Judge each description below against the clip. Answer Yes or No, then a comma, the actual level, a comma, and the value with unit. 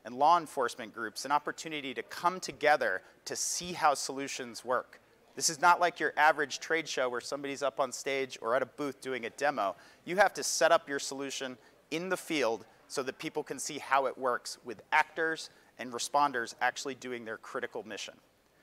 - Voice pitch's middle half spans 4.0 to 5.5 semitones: No, average, 3.4 semitones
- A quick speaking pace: No, average, 195 wpm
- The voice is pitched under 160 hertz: Yes, medium, 140 Hz